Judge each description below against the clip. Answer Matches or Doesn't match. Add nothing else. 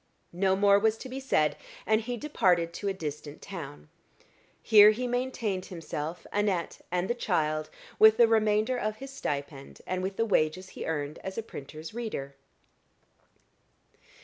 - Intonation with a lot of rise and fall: Matches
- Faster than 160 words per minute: Doesn't match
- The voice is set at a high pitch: Matches